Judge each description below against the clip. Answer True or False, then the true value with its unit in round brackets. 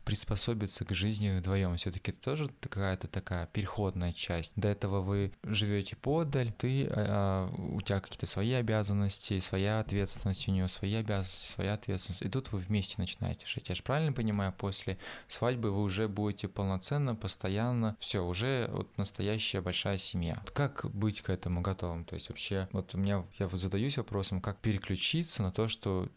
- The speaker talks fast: True (170 wpm)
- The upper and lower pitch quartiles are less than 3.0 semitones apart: True (2.6 semitones)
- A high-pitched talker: False (100 Hz)